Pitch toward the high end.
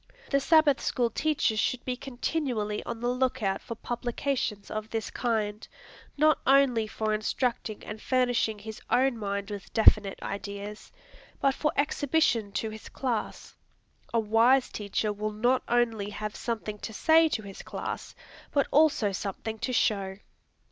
Yes: high, 225 Hz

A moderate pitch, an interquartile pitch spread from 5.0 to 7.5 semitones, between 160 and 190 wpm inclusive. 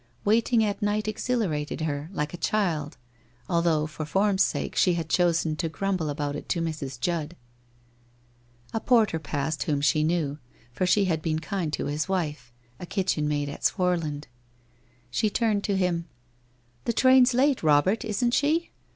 Yes: medium, 170 Hz; wide, 5.4 semitones; average, 170 wpm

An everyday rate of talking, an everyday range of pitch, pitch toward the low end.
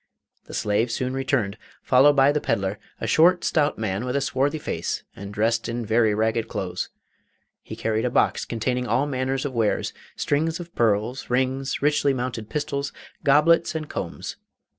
Yes: average, 165 wpm; average, 4.4 semitones; low, 130 Hz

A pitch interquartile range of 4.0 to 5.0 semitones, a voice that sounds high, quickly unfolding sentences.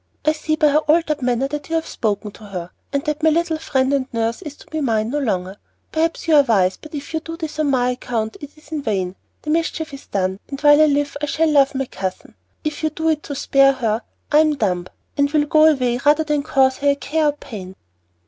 Yes: average, 4.5 semitones; very high, 285 Hz; fast, 250 wpm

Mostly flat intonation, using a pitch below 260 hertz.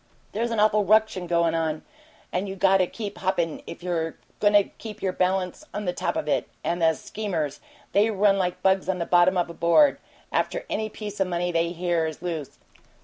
No: average, 3.3 semitones; medium, 185 Hz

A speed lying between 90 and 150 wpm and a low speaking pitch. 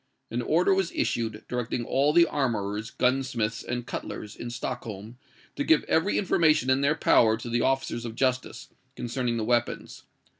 No: average, 160 wpm; low, 125 Hz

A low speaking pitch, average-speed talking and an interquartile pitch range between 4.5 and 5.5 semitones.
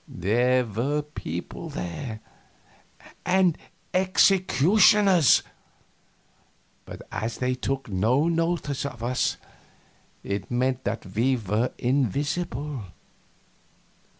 No: low, 130 Hz; slow, 85 wpm; average, 5.0 semitones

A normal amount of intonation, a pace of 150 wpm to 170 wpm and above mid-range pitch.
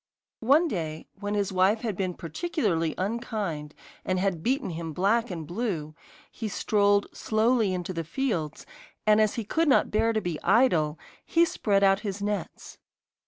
Yes: average, 4.6 semitones; average, 165 wpm; high, 200 Hz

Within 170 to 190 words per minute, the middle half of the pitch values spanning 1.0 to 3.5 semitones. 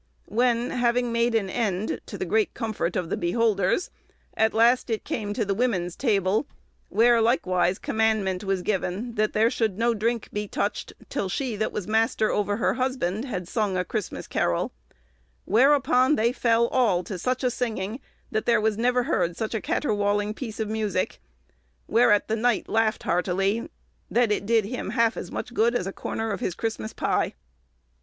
Yes: average, 180 wpm; average, 2.9 semitones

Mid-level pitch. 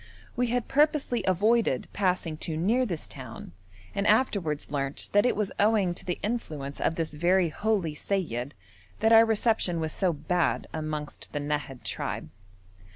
Yes: medium, 180 Hz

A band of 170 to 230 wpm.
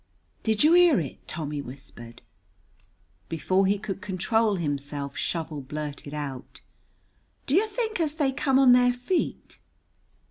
No: slow, 135 wpm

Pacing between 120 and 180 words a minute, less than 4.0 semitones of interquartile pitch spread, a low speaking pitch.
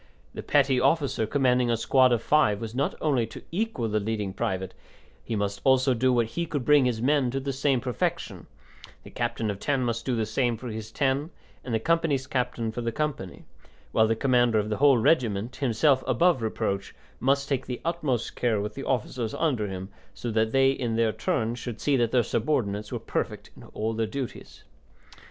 No: fast, 205 wpm; average, 3.4 semitones; low, 120 Hz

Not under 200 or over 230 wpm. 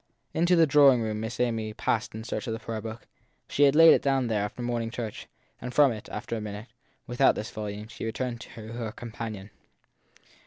Yes: fast, 205 wpm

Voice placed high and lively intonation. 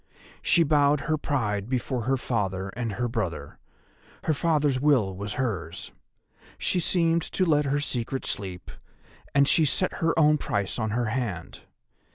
No: low, 130 Hz; wide, 6.0 semitones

